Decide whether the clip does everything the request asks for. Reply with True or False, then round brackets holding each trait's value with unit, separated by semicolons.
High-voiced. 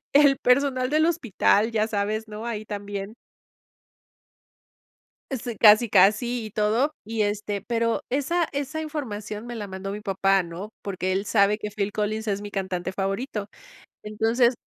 True (215 Hz)